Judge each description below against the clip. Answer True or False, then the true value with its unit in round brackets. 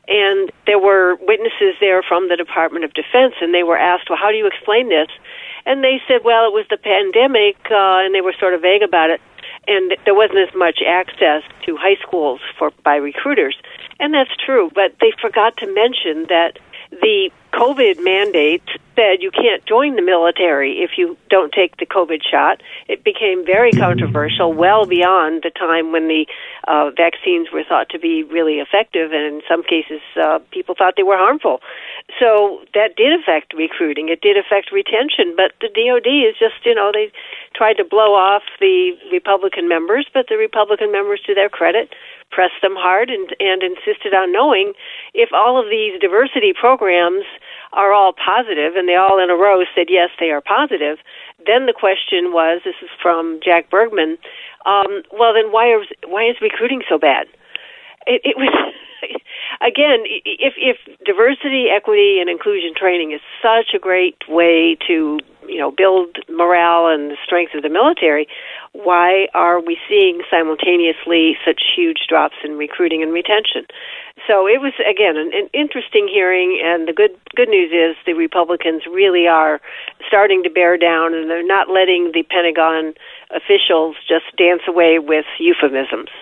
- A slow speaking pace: False (175 wpm)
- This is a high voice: True (200 Hz)